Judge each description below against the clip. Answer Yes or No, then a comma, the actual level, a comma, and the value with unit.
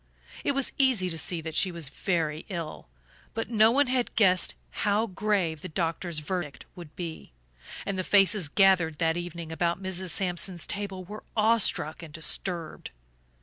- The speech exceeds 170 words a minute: No, average, 160 wpm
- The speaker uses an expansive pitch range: No, average, 3.8 semitones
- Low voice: No, medium, 180 Hz